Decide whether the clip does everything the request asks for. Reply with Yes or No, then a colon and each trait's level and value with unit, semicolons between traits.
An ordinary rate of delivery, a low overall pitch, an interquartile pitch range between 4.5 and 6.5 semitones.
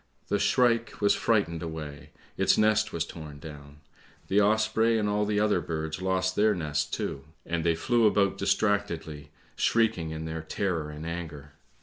Yes: average, 160 wpm; very low, 90 Hz; average, 4.8 semitones